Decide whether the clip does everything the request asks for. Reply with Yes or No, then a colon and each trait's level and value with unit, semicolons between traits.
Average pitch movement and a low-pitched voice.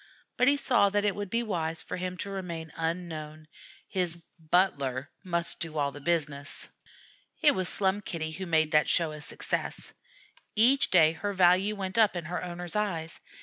No: average, 3.6 semitones; medium, 175 Hz